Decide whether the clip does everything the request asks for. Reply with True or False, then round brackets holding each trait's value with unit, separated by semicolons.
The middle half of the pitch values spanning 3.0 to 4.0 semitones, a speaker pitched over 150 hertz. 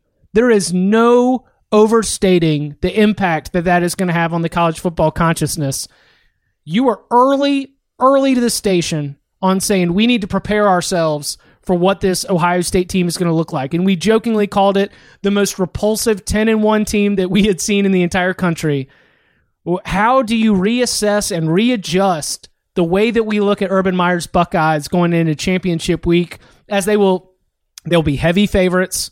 True (3.5 semitones; 190 Hz)